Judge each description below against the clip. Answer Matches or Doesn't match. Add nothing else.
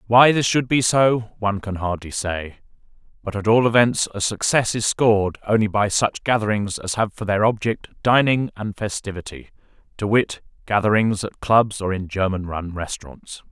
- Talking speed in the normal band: Matches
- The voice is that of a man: Matches